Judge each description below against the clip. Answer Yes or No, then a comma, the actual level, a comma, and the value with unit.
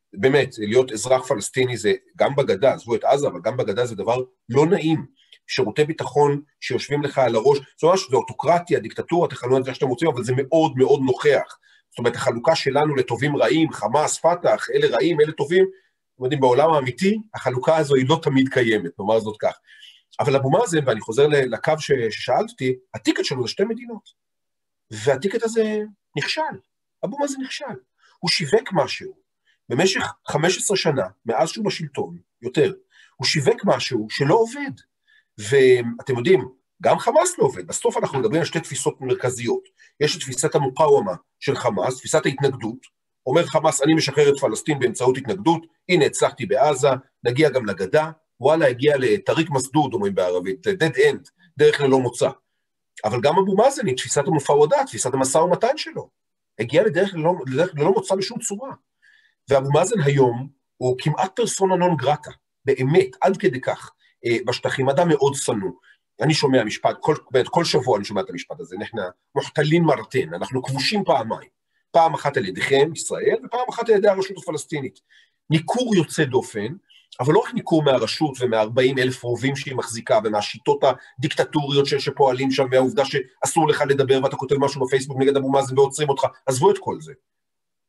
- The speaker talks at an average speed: No, fast, 160 wpm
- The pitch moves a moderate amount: No, wide, 7.3 semitones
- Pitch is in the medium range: Yes, medium, 155 Hz